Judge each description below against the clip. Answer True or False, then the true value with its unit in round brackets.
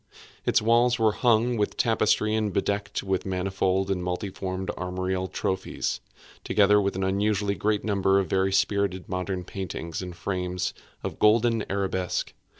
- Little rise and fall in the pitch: True (2.2 semitones)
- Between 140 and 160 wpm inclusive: True (150 wpm)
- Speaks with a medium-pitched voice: False (95 Hz)